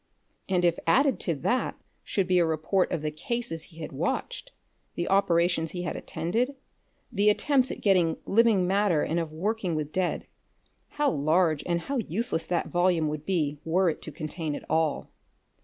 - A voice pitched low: No, medium, 175 Hz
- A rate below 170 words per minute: No, average, 175 wpm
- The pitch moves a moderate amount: Yes, average, 3.9 semitones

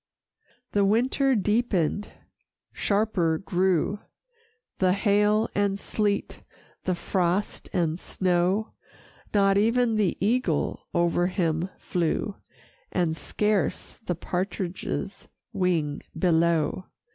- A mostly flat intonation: No, average, 3.1 semitones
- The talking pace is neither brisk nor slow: No, slow, 95 wpm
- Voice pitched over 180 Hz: Yes, high, 190 Hz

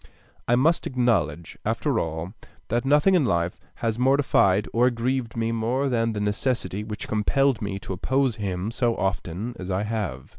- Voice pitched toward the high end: No, low, 115 Hz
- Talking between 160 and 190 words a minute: Yes, average, 170 wpm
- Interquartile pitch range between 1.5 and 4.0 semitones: No, average, 4.5 semitones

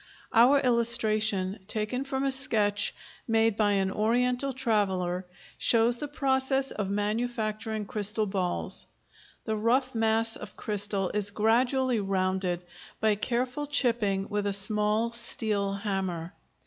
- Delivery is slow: Yes, slow, 120 wpm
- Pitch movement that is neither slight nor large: Yes, average, 3.2 semitones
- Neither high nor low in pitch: No, high, 215 Hz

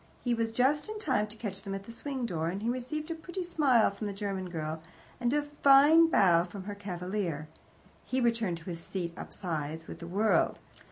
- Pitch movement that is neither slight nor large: No, wide, 6.6 semitones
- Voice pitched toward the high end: Yes, high, 210 Hz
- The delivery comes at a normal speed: No, fast, 215 wpm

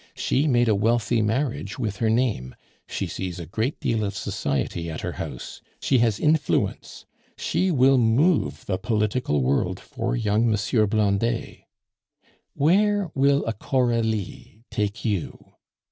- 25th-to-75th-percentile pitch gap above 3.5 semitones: Yes, average, 4.4 semitones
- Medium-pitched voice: No, low, 115 Hz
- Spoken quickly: No, average, 140 wpm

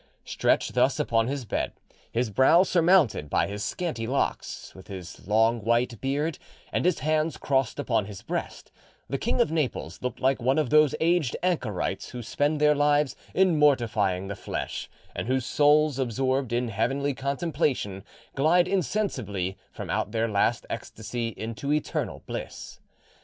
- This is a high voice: No, low, 130 Hz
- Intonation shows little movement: No, average, 5.1 semitones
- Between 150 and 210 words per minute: Yes, average, 155 wpm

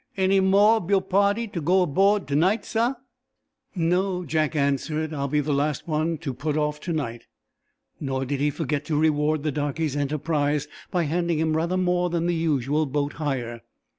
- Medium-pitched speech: Yes, medium, 155 Hz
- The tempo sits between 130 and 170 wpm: No, average, 185 wpm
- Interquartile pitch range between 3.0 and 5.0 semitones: Yes, average, 3.5 semitones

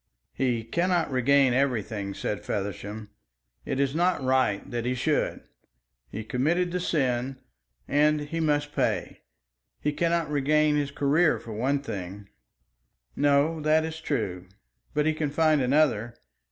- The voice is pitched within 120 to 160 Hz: Yes, medium, 140 Hz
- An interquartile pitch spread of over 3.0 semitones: Yes, average, 4.2 semitones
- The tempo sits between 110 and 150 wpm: Yes, average, 140 wpm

